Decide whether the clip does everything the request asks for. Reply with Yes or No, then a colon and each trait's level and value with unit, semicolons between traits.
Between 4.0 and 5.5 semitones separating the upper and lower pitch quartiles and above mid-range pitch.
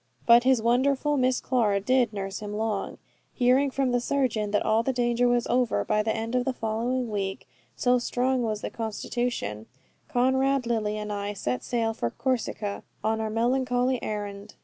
No: average, 3.1 semitones; high, 235 Hz